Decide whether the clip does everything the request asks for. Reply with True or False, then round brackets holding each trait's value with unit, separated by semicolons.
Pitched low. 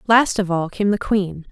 False (195 Hz)